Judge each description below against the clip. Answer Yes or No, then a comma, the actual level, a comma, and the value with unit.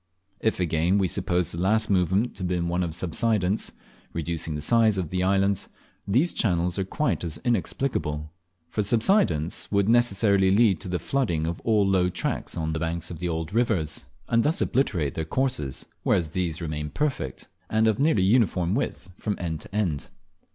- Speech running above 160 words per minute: Yes, average, 180 wpm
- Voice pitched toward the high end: No, very low, 90 Hz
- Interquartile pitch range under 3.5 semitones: No, average, 4.8 semitones